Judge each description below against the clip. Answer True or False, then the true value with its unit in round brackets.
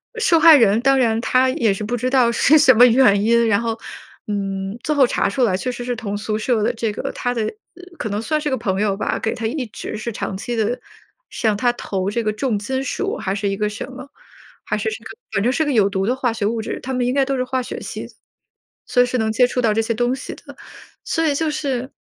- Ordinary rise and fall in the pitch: True (3.4 semitones)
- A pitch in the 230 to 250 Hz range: True (235 Hz)